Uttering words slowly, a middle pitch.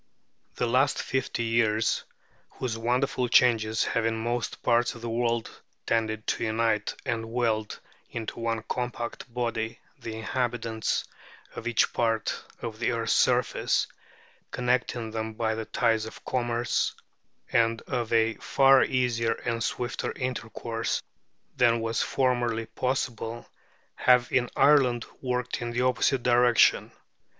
No: slow, 130 wpm; low, 115 Hz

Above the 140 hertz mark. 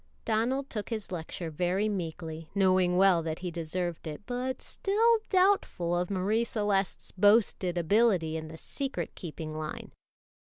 Yes: medium, 185 Hz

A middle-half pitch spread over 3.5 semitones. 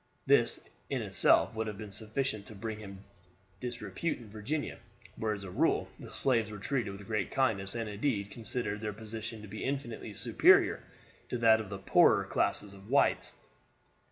No: narrow, 2.5 semitones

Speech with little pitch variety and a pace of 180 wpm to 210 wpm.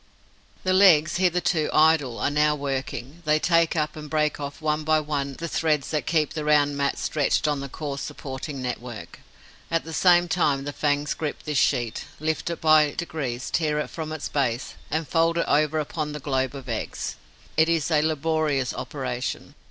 Yes: narrow, 2.1 semitones; average, 185 wpm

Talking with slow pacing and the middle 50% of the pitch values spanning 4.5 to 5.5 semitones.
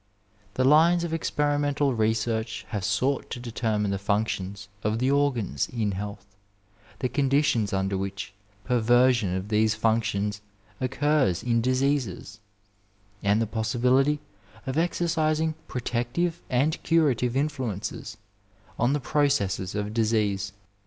Yes: slow, 125 wpm; average, 5.2 semitones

